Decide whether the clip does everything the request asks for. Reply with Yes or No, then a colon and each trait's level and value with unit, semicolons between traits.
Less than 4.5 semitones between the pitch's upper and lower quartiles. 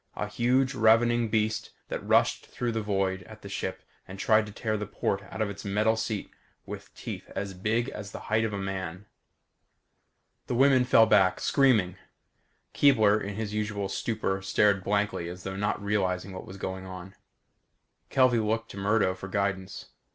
Yes: narrow, 2.6 semitones